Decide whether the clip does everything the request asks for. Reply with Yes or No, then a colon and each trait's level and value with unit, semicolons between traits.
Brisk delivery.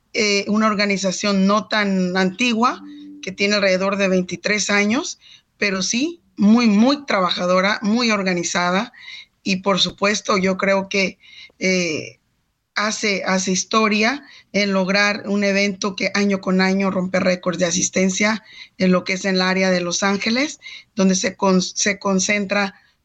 No: average, 145 wpm